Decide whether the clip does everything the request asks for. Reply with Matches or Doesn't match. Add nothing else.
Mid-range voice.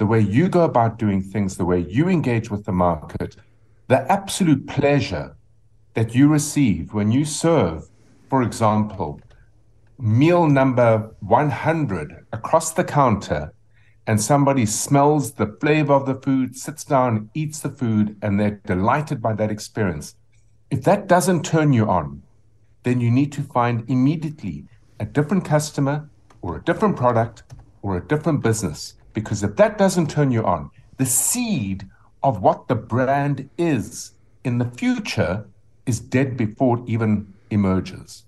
Doesn't match